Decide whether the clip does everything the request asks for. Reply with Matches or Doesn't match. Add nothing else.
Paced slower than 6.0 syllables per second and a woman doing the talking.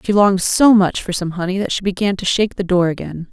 Doesn't match